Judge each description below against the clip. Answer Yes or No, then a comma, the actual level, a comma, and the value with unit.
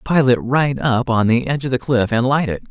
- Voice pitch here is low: Yes, low, 125 Hz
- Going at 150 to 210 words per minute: No, fast, 290 wpm